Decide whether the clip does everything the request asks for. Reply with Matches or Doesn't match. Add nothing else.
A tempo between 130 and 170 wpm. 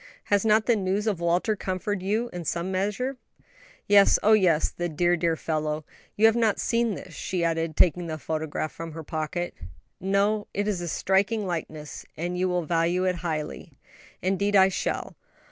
Doesn't match